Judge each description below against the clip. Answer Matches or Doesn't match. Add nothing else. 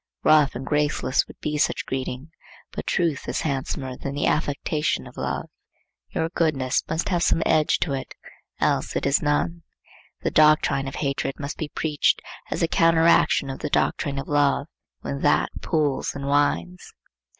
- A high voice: Doesn't match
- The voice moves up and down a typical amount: Doesn't match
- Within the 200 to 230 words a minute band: Doesn't match